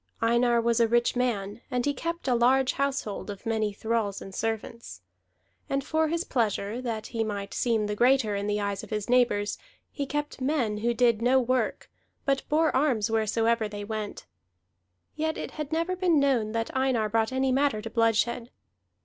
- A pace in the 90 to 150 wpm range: No, average, 185 wpm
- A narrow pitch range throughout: No, average, 3.7 semitones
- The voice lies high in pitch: Yes, high, 235 Hz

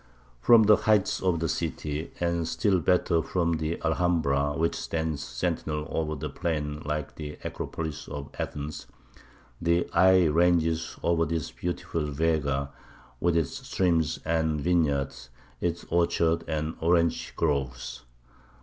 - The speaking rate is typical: No, slow, 130 wpm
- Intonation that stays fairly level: Yes, narrow, 2.2 semitones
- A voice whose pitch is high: No, very low, 80 Hz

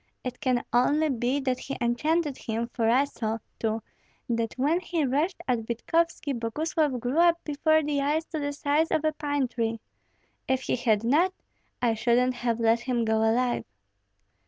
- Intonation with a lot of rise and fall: No, average, 4.3 semitones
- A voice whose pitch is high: Yes, very high, 255 Hz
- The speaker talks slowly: No, average, 175 wpm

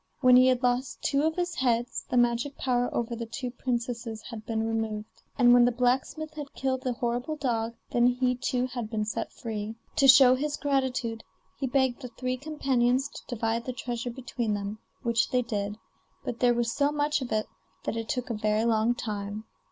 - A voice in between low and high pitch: No, high, 245 Hz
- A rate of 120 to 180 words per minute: No, average, 200 wpm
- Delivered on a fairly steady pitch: Yes, narrow, 2.3 semitones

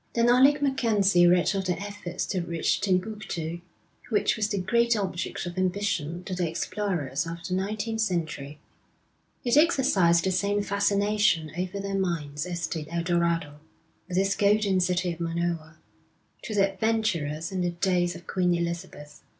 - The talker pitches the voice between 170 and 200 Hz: Yes, medium, 185 Hz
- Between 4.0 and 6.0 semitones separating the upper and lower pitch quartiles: No, average, 3.2 semitones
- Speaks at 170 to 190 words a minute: No, average, 160 wpm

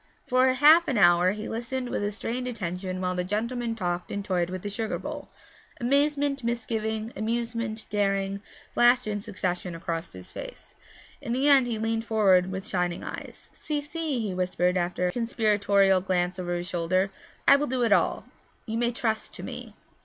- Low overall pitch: No, high, 215 Hz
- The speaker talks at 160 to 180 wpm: Yes, average, 175 wpm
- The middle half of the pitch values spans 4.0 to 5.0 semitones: Yes, average, 4.6 semitones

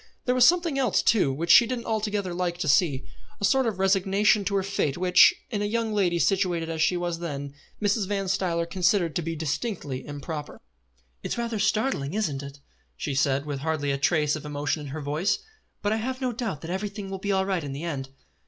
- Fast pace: Yes, fast, 225 wpm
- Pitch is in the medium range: Yes, medium, 180 Hz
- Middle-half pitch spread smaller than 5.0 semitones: No, wide, 5.6 semitones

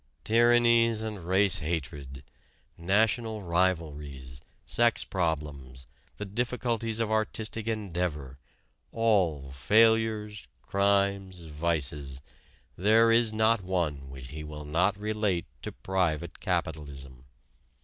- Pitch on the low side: Yes, very low, 95 Hz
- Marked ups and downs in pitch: Yes, wide, 6.5 semitones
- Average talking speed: No, slow, 100 wpm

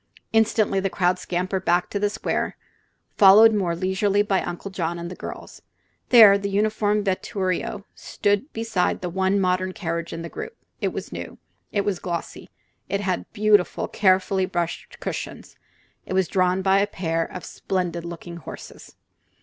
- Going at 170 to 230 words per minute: No, average, 160 wpm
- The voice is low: No, high, 190 Hz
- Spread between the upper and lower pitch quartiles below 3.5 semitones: Yes, narrow, 2.4 semitones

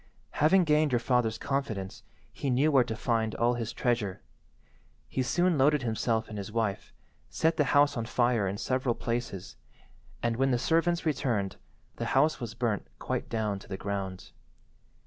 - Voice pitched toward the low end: Yes, low, 120 Hz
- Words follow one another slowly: No, average, 165 wpm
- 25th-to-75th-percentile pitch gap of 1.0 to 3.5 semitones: No, average, 4.2 semitones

